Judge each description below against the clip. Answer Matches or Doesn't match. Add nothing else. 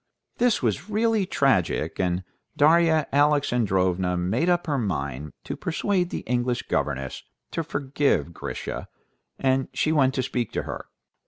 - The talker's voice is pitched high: Doesn't match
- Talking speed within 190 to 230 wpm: Doesn't match